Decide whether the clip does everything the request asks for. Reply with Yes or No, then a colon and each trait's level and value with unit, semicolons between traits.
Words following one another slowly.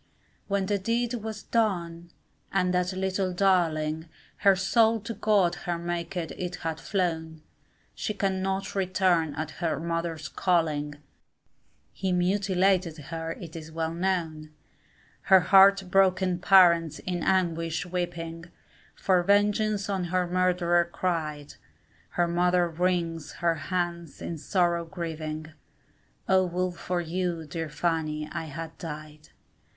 Yes: slow, 125 wpm